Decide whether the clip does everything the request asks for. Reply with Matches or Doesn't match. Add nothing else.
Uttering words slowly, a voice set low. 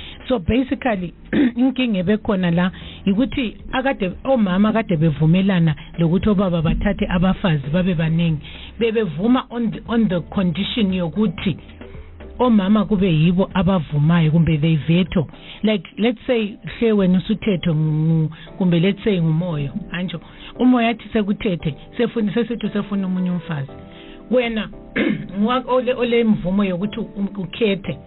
Doesn't match